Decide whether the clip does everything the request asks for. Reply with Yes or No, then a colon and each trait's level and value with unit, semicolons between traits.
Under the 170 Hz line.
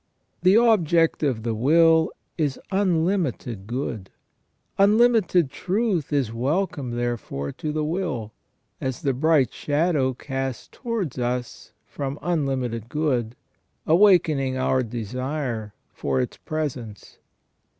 Yes: medium, 140 Hz